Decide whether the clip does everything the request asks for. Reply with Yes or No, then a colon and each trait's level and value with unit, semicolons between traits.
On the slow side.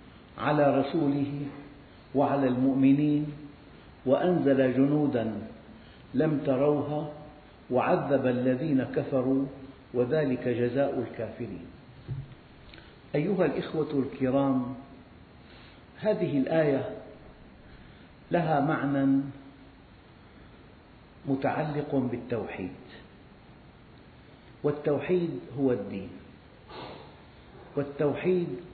Yes: slow, 55 wpm